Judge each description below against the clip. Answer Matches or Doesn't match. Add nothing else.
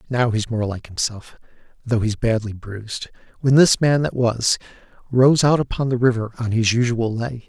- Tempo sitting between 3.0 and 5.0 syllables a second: Matches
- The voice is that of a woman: Doesn't match